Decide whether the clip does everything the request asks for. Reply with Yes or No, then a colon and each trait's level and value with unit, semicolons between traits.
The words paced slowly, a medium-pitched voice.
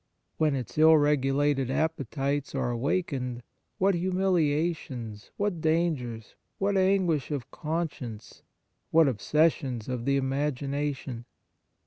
Yes: slow, 110 wpm; medium, 145 Hz